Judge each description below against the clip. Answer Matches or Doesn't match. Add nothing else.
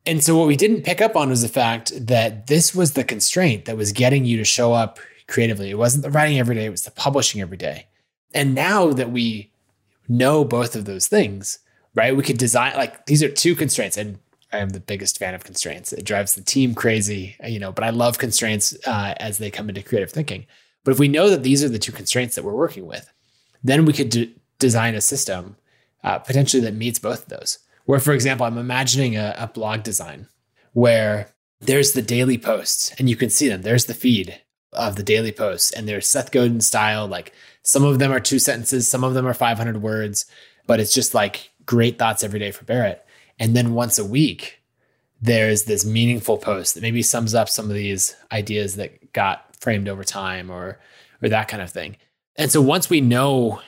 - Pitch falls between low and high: Doesn't match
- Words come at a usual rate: Doesn't match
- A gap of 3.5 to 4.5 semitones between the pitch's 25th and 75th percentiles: Matches